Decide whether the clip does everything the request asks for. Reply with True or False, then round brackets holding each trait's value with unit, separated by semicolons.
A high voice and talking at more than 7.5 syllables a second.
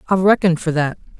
False (175 Hz; 8.2 syllables/s)